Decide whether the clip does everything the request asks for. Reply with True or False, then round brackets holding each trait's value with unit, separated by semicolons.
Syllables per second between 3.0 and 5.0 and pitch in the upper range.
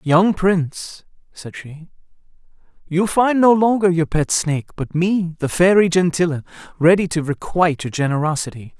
False (4.9 syllables/s; 170 Hz)